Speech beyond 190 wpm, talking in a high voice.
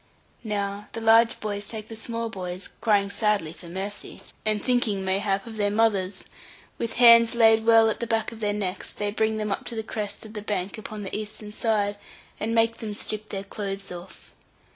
Yes: average, 200 wpm; high, 210 Hz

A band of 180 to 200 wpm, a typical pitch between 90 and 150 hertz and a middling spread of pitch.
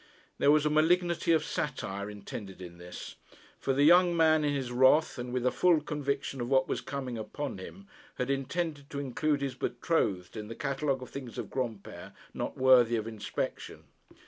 Yes: average, 185 wpm; low, 135 Hz; average, 4.2 semitones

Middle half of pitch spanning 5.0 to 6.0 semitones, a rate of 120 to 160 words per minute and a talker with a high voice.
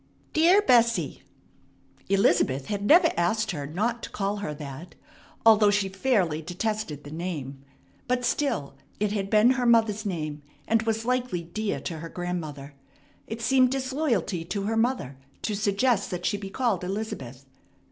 Yes: wide, 5.4 semitones; average, 155 wpm; high, 205 Hz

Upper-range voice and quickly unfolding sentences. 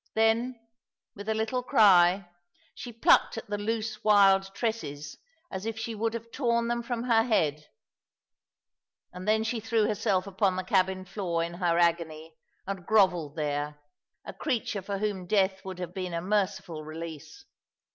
No: high, 195 Hz; average, 160 wpm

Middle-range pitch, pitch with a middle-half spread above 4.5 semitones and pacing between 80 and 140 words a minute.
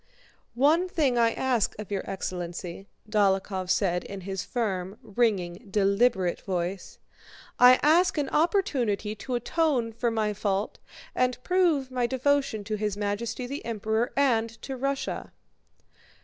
No: high, 225 Hz; average, 4.9 semitones; slow, 135 wpm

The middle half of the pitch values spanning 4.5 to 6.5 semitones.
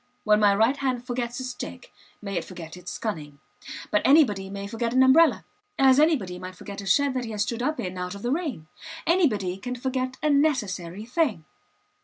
Yes: wide, 5.4 semitones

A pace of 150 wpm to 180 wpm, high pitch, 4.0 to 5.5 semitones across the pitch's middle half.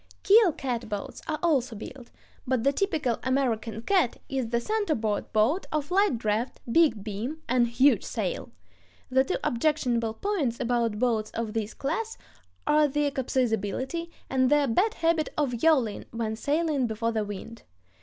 Yes: average, 155 wpm; very high, 255 Hz; average, 5.1 semitones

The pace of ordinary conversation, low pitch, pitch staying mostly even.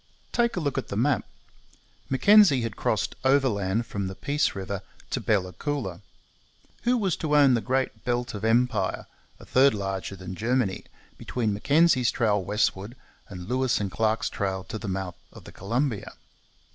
No: average, 165 wpm; low, 115 Hz; average, 5.3 semitones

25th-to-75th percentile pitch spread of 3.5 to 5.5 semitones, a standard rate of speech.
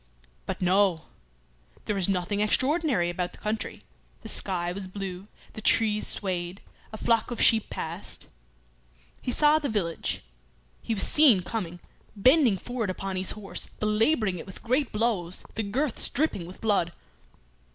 Yes: average, 3.9 semitones; average, 150 wpm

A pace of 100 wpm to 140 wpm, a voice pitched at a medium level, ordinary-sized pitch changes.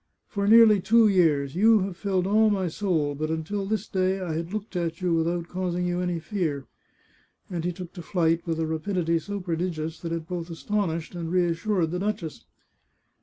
No: average, 190 wpm; medium, 175 Hz; average, 3.2 semitones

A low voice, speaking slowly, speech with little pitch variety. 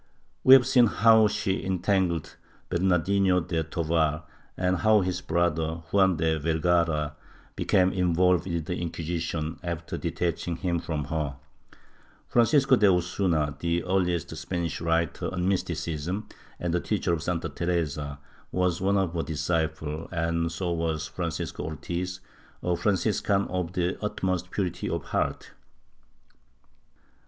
Yes: very low, 85 Hz; slow, 130 wpm; narrow, 2.3 semitones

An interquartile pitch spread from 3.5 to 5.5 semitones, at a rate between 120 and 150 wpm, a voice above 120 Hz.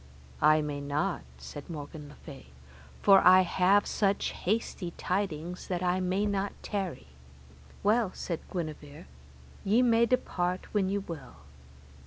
Yes: average, 4.3 semitones; slow, 135 wpm; medium, 185 Hz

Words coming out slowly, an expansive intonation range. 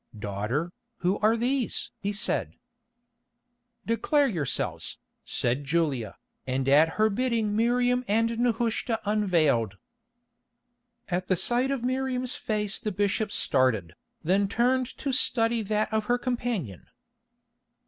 Yes: slow, 115 wpm; wide, 7.0 semitones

